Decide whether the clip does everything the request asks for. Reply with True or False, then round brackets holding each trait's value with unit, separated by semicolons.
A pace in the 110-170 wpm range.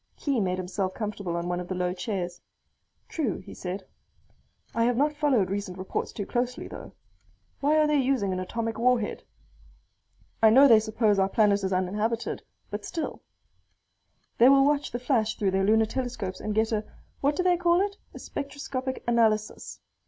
False (180 wpm)